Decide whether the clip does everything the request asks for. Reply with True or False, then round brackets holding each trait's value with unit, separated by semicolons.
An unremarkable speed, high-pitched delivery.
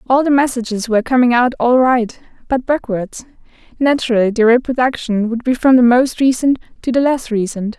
True (175 wpm; 245 Hz)